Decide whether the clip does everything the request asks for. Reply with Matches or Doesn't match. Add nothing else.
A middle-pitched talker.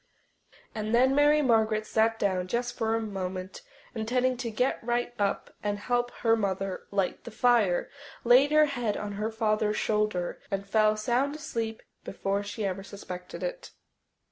Doesn't match